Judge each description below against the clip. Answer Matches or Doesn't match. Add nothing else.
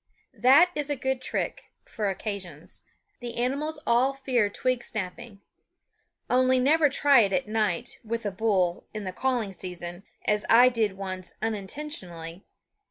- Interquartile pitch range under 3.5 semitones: Doesn't match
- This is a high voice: Matches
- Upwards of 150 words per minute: Doesn't match